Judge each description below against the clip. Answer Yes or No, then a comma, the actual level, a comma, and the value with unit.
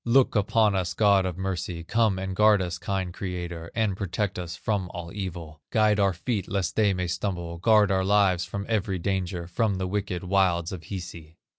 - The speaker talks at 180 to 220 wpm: Yes, average, 190 wpm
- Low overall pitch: Yes, very low, 95 Hz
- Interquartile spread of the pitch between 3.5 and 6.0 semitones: No, narrow, 2.6 semitones